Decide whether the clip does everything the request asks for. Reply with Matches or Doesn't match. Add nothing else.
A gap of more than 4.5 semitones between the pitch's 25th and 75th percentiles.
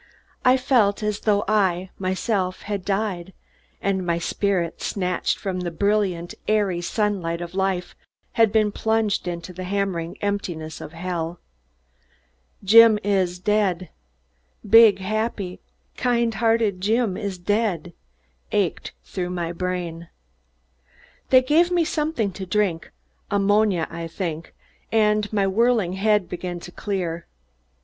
Doesn't match